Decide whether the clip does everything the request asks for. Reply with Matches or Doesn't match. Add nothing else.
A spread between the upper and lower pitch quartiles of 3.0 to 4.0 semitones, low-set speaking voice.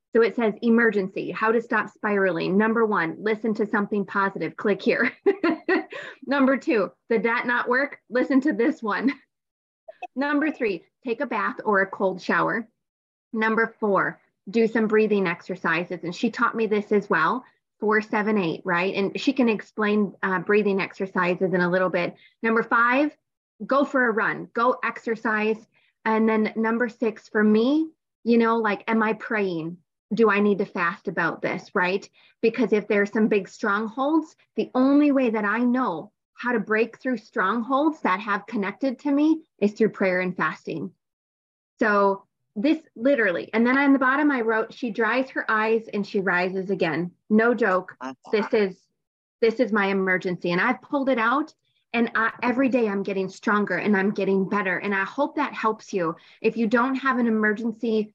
Doesn't match